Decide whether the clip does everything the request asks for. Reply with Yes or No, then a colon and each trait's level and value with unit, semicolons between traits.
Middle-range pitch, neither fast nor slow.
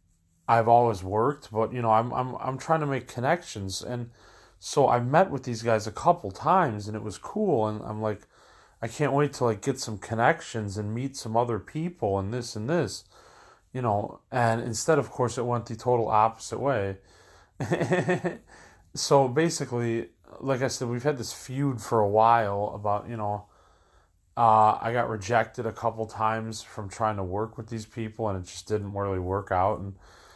No: low, 115 Hz; average, 190 wpm